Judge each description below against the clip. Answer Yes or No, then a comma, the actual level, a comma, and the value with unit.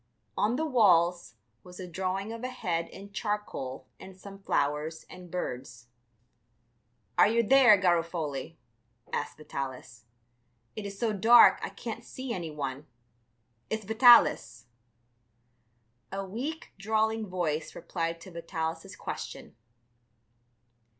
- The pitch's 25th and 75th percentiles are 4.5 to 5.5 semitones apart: Yes, average, 5.1 semitones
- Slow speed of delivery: Yes, slow, 115 wpm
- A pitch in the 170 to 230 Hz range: Yes, medium, 185 Hz